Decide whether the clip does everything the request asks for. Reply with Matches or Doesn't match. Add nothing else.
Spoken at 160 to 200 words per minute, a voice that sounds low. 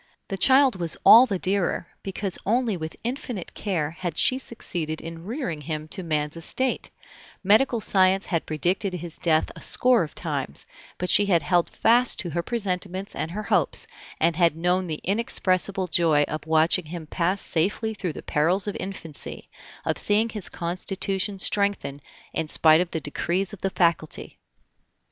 Doesn't match